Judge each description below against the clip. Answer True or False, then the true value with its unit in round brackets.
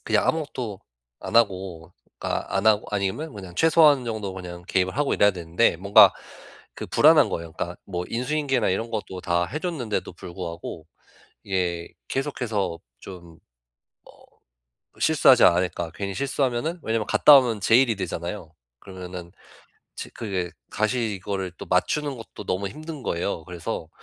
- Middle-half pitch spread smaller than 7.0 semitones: True (5.5 semitones)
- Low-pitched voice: True (100 Hz)